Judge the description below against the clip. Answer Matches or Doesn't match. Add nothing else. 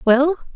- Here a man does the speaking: Doesn't match